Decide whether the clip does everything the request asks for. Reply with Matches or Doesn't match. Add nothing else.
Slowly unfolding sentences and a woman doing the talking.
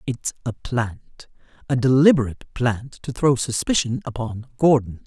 Matches